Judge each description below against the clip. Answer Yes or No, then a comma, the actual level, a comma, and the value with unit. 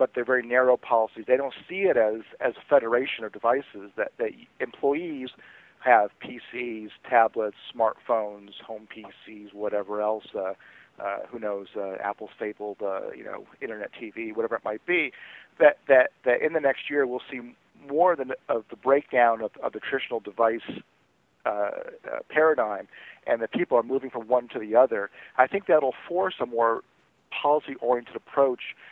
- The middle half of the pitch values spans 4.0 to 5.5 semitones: Yes, average, 4.7 semitones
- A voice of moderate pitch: No, low, 125 Hz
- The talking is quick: No, average, 170 wpm